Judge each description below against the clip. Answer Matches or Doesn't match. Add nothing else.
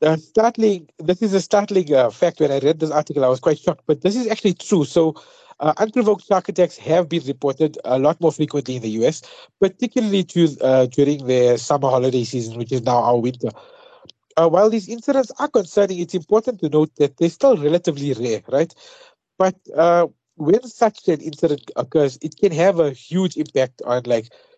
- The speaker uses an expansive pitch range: Matches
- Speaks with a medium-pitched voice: Matches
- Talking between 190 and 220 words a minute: Matches